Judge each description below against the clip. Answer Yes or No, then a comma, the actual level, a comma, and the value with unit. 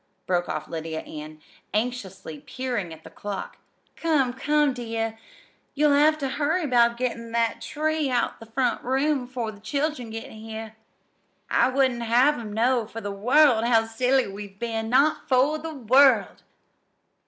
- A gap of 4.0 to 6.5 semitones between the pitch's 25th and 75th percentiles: No, average, 3.6 semitones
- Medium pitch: No, high, 240 Hz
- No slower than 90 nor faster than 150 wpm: No, average, 160 wpm